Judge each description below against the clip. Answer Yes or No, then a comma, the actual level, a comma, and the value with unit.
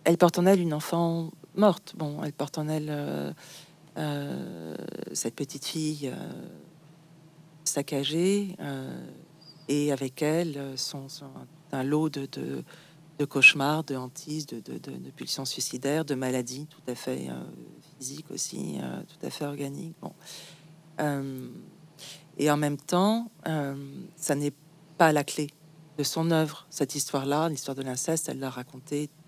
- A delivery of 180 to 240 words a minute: No, average, 155 wpm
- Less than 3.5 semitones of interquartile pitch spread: Yes, narrow, 2.5 semitones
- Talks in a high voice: No, medium, 150 Hz